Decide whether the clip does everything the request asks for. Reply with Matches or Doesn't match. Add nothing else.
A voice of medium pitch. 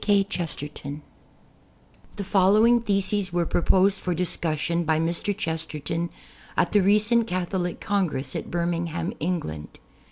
Matches